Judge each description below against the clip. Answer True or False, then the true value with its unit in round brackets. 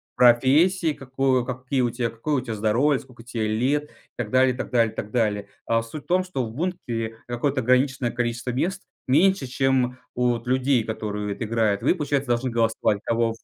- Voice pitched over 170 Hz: False (125 Hz)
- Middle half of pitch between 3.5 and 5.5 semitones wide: False (2.8 semitones)